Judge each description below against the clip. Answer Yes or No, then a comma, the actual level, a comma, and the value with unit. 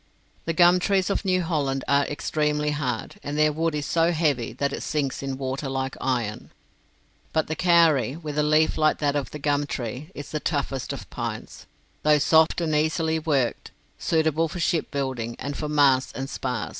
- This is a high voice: No, medium, 150 Hz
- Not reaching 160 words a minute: No, average, 185 wpm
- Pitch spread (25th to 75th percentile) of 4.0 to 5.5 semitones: No, average, 2.8 semitones